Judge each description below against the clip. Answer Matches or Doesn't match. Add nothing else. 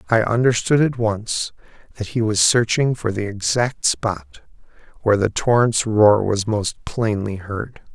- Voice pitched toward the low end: Matches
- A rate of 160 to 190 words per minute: Doesn't match